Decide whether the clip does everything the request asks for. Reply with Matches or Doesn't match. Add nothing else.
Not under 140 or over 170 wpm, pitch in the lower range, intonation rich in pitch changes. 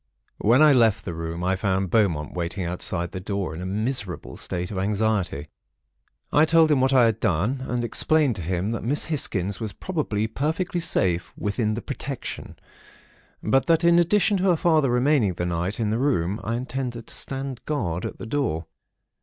Doesn't match